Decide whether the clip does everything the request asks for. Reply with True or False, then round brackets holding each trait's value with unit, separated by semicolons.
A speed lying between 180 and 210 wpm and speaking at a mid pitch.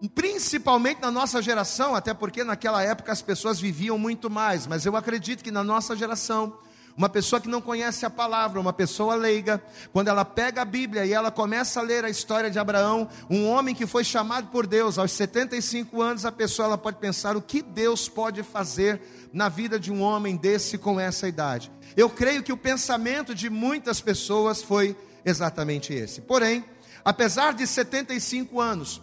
False (185 wpm; 220 Hz)